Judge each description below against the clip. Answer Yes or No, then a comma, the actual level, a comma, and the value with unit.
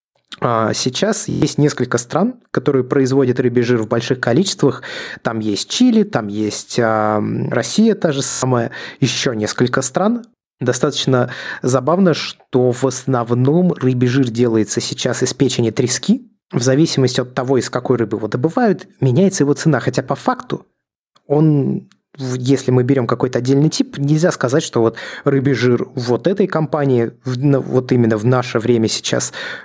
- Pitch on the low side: Yes, low, 130 Hz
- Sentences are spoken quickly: No, average, 145 wpm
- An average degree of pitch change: Yes, average, 3.5 semitones